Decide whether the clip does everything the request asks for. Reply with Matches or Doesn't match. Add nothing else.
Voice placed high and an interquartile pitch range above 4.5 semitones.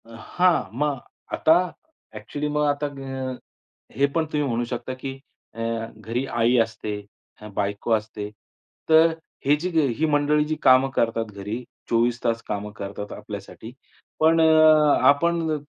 Doesn't match